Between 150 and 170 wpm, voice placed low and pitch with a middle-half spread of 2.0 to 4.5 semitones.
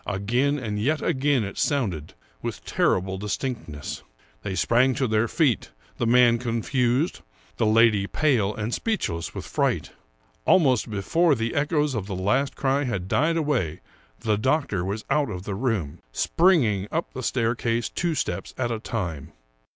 No: average, 155 wpm; low, 115 Hz; wide, 5.6 semitones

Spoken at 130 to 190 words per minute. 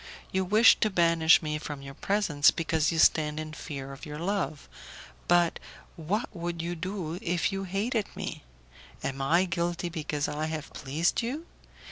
Yes: average, 165 wpm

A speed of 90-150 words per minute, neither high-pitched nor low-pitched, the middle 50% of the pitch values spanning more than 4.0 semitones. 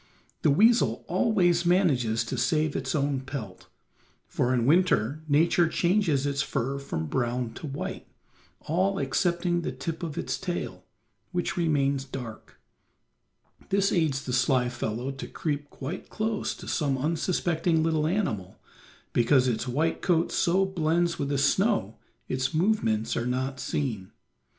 Yes: average, 140 wpm; medium, 145 Hz; average, 5.2 semitones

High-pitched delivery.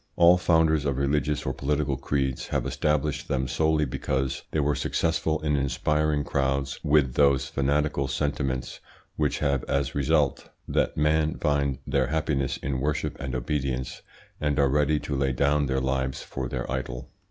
No: very low, 70 Hz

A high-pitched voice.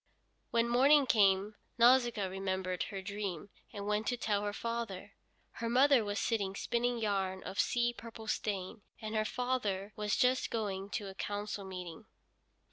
Yes: high, 210 Hz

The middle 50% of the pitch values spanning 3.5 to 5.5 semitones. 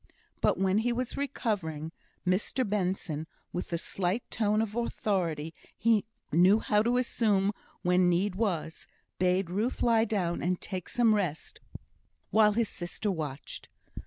Yes: average, 3.9 semitones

